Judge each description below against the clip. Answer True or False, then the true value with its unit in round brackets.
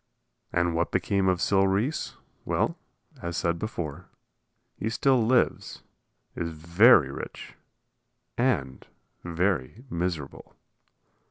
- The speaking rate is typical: False (100 wpm)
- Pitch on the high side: False (90 Hz)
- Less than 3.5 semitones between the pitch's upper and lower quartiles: False (4.5 semitones)